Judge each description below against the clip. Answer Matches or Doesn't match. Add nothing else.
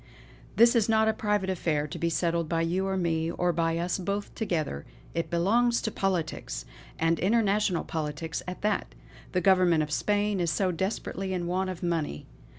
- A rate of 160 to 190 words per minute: Matches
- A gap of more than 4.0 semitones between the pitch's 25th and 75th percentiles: Doesn't match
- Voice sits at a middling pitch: Matches